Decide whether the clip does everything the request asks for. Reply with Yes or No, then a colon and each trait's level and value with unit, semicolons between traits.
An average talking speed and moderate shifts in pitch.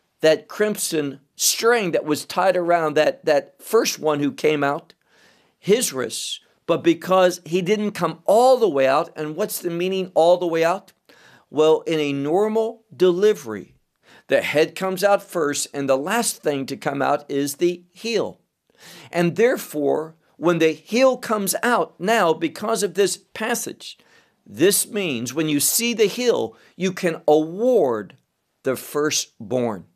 No: average, 155 wpm; wide, 5.8 semitones